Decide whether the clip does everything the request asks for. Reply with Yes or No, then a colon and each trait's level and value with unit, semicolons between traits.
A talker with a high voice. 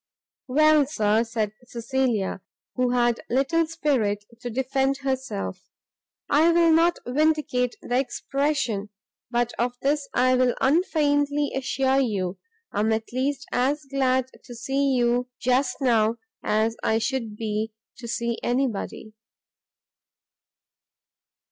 Yes: very high, 255 Hz